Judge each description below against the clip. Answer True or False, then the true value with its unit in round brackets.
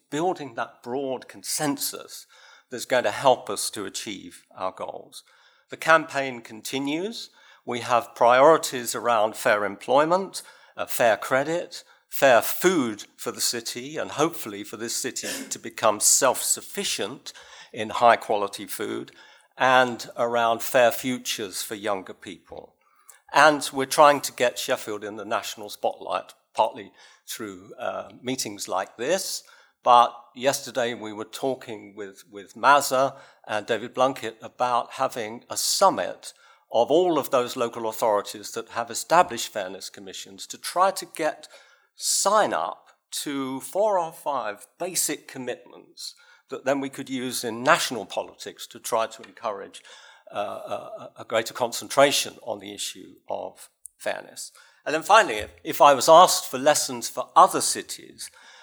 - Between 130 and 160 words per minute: True (140 wpm)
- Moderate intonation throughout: True (3.8 semitones)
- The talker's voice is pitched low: True (130 Hz)